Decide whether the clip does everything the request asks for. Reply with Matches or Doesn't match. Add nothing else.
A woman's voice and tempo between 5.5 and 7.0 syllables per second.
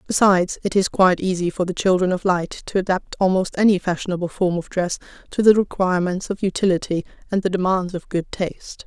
Matches